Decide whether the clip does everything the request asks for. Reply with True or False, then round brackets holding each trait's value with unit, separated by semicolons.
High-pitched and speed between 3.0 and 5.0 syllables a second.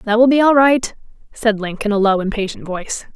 False (225 Hz; 5.6 syllables/s)